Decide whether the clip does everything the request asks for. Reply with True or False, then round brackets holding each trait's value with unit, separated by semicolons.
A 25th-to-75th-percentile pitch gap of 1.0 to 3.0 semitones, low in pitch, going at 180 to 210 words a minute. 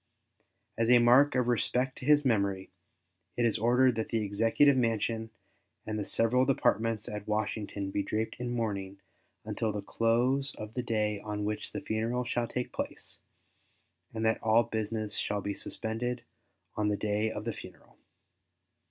False (2.5 semitones; 110 Hz; 160 wpm)